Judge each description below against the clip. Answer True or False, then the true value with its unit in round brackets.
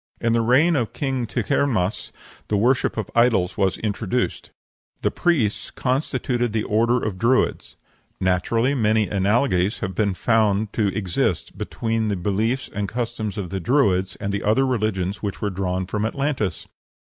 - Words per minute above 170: False (155 wpm)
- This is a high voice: False (110 Hz)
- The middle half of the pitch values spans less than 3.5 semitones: False (3.8 semitones)